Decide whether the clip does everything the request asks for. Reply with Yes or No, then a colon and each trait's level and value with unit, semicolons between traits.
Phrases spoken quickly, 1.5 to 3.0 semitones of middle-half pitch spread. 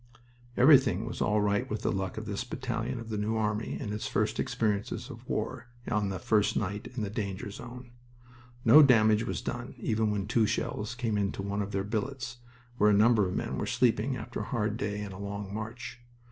Yes: fast, 210 wpm; narrow, 2.5 semitones